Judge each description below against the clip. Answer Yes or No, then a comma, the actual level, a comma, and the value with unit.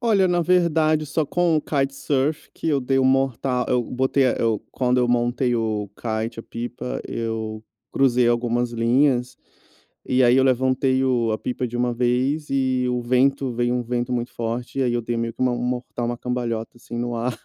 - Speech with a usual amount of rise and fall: No, narrow, 2.0 semitones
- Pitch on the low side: Yes, low, 125 Hz